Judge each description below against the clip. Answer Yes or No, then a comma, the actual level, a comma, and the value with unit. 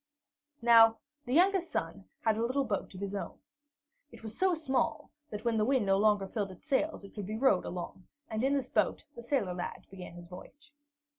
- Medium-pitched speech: No, high, 220 Hz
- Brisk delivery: Yes, fast, 210 wpm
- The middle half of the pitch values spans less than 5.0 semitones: No, wide, 5.4 semitones